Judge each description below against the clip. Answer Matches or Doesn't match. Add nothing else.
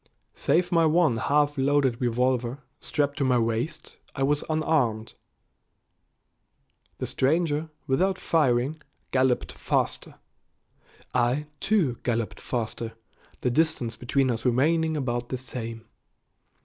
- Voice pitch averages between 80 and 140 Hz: Matches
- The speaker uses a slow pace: Matches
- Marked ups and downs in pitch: Doesn't match